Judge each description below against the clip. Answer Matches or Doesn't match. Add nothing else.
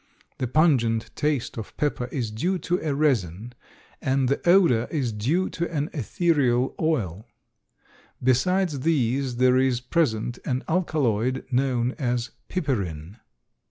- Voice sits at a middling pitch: Doesn't match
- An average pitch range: Matches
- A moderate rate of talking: Doesn't match